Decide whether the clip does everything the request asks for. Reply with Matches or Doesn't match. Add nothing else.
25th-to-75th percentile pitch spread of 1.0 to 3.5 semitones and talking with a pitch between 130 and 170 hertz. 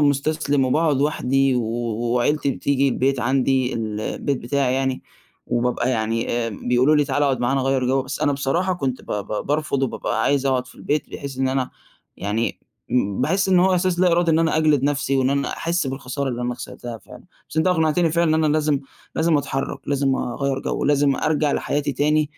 Matches